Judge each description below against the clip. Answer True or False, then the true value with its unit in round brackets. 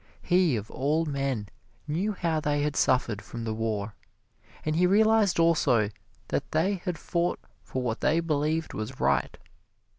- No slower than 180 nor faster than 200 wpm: False (155 wpm)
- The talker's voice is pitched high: False (150 Hz)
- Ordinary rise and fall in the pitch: False (5.8 semitones)